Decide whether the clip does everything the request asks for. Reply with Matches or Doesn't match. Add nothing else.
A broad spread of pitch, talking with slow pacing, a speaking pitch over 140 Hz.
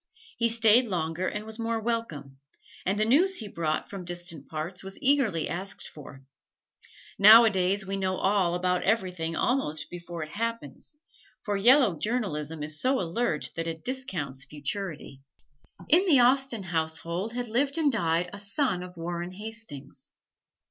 Doesn't match